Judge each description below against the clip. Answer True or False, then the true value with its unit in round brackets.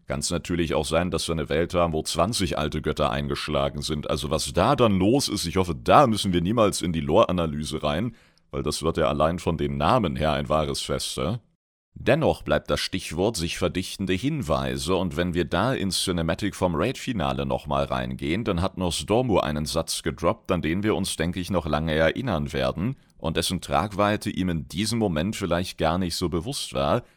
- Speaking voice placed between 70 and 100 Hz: True (85 Hz)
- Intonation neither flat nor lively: True (3.6 semitones)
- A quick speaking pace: True (200 wpm)